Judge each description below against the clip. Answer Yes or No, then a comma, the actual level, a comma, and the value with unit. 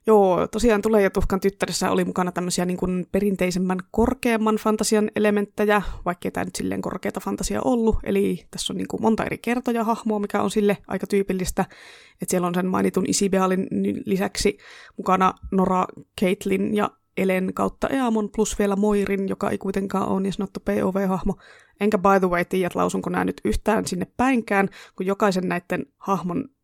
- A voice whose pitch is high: Yes, high, 195 Hz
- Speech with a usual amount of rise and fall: No, narrow, 2.2 semitones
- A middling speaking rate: No, fast, 170 wpm